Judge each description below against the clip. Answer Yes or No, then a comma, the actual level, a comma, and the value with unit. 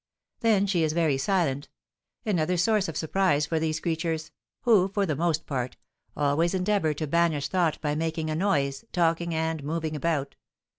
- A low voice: No, medium, 160 Hz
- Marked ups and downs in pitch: No, average, 3.0 semitones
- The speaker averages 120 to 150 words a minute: No, average, 165 wpm